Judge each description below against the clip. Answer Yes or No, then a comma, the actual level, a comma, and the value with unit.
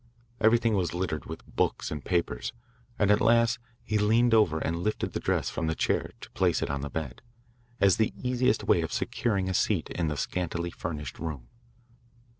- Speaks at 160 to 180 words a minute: No, average, 190 wpm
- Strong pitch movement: Yes, wide, 5.7 semitones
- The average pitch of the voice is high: No, very low, 90 Hz